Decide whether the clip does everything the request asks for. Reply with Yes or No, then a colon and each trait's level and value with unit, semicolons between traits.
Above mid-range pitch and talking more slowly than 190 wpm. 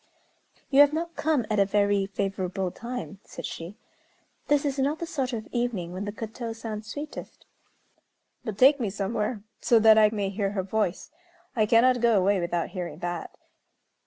Yes: high, 215 Hz; average, 175 wpm